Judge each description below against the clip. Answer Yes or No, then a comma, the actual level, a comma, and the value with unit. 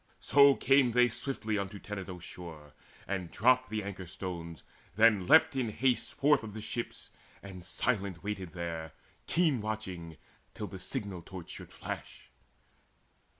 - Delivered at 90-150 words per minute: Yes, average, 145 wpm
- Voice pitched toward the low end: Yes, low, 100 Hz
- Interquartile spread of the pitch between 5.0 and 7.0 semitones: Yes, average, 5.3 semitones